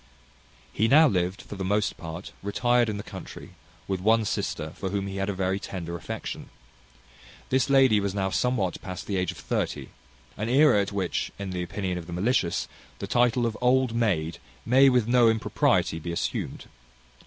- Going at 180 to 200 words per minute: Yes, average, 185 wpm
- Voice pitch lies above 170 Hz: No, low, 100 Hz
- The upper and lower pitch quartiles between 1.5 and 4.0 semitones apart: No, average, 4.6 semitones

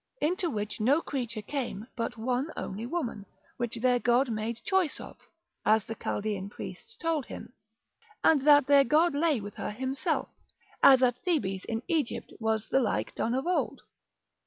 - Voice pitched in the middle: No, very high, 250 Hz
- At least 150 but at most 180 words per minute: Yes, average, 165 wpm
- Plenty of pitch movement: No, average, 4.9 semitones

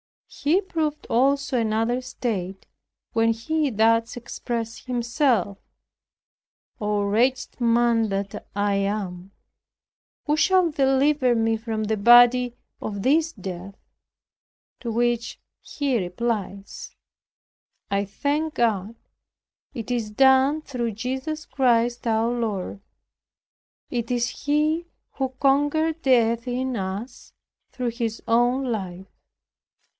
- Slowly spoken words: Yes, slow, 105 wpm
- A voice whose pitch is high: Yes, high, 235 Hz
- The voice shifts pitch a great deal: No, average, 3.4 semitones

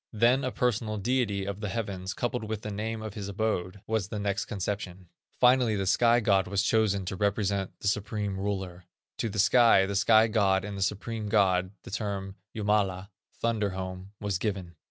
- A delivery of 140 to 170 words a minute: No, average, 185 wpm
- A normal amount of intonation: No, narrow, 2.3 semitones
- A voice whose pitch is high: No, low, 100 Hz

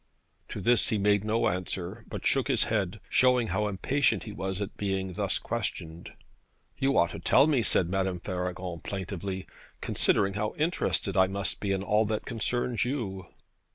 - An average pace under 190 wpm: Yes, average, 170 wpm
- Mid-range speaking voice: No, low, 100 Hz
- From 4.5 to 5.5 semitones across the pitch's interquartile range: No, average, 3.5 semitones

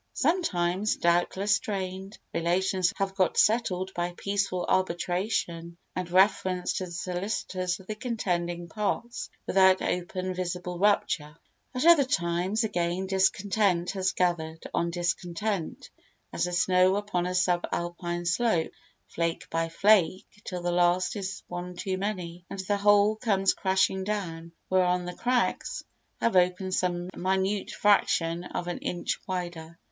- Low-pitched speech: No, medium, 185 Hz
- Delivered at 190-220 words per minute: No, slow, 135 wpm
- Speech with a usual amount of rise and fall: No, narrow, 2.2 semitones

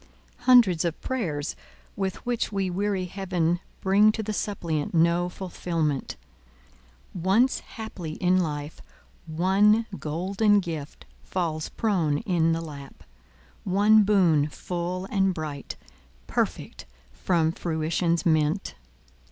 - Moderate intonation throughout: Yes, average, 3.9 semitones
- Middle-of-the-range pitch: Yes, medium, 175 Hz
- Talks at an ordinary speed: No, slow, 110 wpm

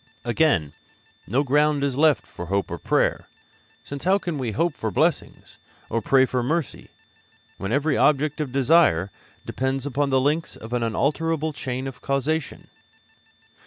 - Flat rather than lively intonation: No, average, 3.6 semitones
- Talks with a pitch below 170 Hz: Yes, medium, 140 Hz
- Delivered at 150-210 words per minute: Yes, average, 155 wpm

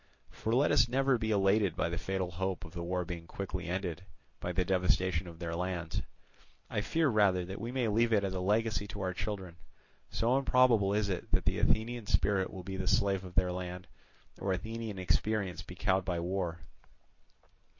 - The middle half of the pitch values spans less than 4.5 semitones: Yes, average, 3.0 semitones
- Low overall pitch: Yes, very low, 95 Hz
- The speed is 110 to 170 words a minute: No, average, 195 wpm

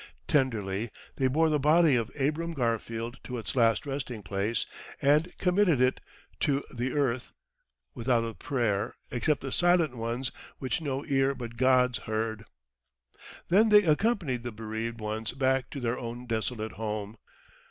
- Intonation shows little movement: No, average, 4.0 semitones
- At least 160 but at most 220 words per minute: No, average, 150 wpm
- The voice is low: Yes, low, 125 Hz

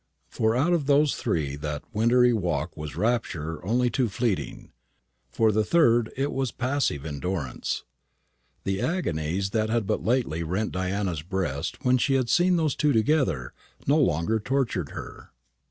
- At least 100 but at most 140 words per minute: No, average, 155 wpm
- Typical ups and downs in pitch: No, wide, 7.2 semitones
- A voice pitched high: No, low, 110 Hz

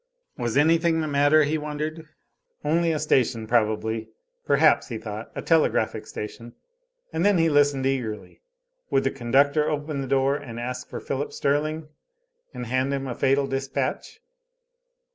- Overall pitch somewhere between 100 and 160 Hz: Yes, medium, 140 Hz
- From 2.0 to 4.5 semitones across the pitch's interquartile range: Yes, average, 3.3 semitones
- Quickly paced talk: No, average, 150 wpm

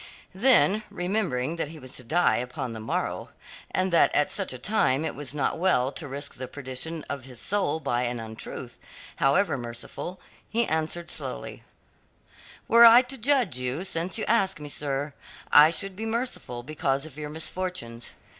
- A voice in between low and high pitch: Yes, medium, 155 Hz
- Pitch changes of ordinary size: No, wide, 6.5 semitones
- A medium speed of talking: Yes, average, 175 wpm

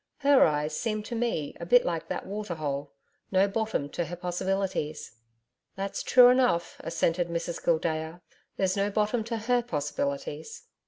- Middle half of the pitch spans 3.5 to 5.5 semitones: Yes, average, 5.1 semitones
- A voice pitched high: No, medium, 175 Hz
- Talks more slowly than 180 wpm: Yes, average, 155 wpm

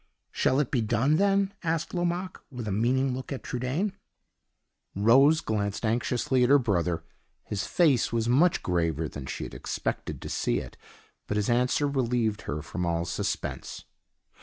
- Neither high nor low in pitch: No, low, 125 Hz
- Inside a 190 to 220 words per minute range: No, average, 160 wpm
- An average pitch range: No, wide, 5.7 semitones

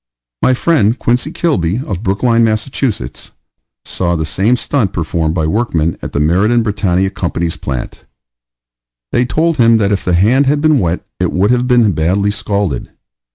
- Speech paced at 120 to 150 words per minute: No, average, 160 wpm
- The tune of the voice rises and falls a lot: Yes, wide, 5.7 semitones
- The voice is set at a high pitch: No, low, 105 Hz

